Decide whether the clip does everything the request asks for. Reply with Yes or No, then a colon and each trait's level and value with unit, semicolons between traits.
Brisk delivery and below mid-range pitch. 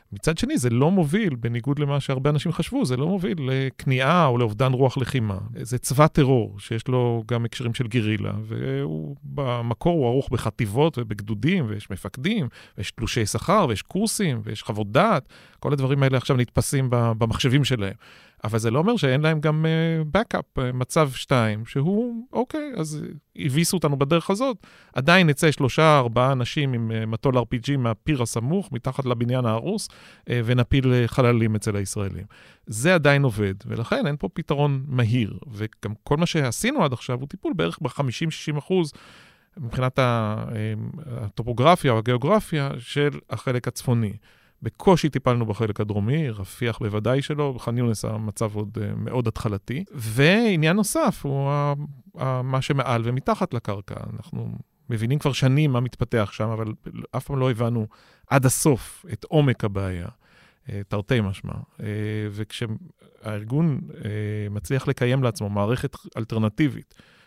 No: average, 140 wpm; low, 125 Hz